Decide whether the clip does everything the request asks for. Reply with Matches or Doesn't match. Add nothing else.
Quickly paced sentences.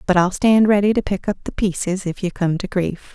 Matches